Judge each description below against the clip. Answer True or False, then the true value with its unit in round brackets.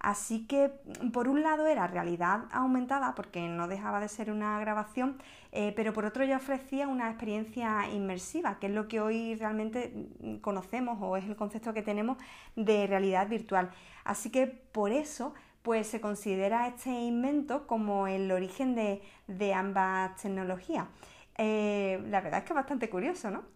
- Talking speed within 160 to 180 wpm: True (165 wpm)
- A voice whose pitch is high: True (215 Hz)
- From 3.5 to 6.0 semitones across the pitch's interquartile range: True (4.2 semitones)